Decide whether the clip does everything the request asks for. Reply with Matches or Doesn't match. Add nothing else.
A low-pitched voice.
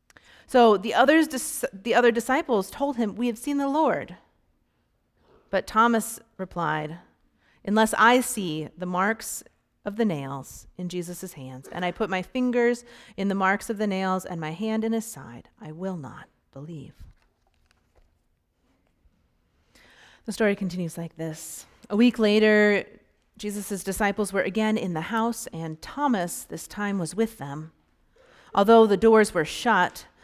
Doesn't match